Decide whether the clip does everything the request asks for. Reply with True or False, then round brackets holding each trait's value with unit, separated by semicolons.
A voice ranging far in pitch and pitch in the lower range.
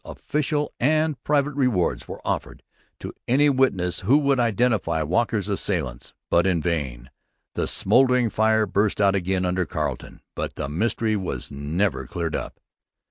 True (6.8 semitones; 105 Hz)